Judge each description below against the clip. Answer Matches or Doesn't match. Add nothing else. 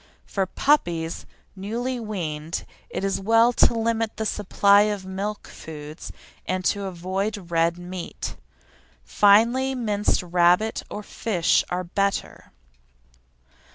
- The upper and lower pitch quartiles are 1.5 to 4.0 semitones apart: Matches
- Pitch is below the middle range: Doesn't match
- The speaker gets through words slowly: Matches